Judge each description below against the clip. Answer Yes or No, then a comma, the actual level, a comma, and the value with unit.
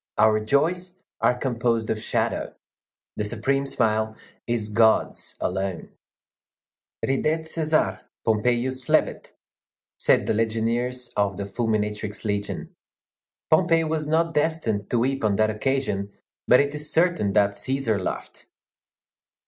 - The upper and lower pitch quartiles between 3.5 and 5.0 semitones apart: Yes, average, 4.7 semitones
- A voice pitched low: Yes, low, 115 Hz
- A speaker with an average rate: No, slow, 120 wpm